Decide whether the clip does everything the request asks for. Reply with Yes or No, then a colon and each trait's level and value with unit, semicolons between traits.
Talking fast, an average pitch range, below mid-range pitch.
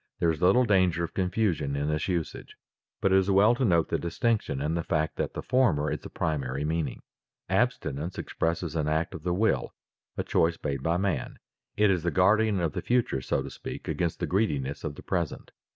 Yes: fast, 210 wpm; average, 4.1 semitones; very low, 85 Hz